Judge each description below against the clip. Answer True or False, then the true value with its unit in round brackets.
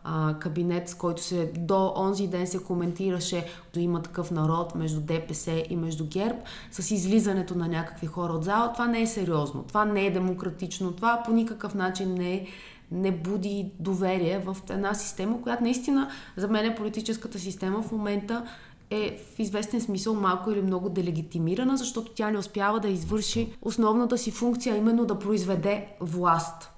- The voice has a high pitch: True (195 Hz)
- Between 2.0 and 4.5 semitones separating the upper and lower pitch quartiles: True (3.6 semitones)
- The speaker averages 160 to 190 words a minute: True (165 wpm)